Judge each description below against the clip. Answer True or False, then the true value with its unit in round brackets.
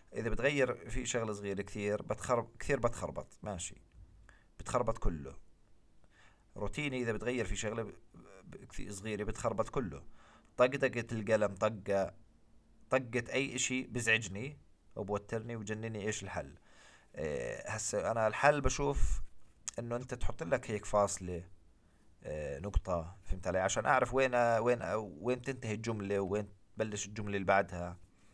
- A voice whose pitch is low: True (105 Hz)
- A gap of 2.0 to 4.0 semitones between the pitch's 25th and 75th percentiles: True (3.2 semitones)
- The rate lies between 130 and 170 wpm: True (140 wpm)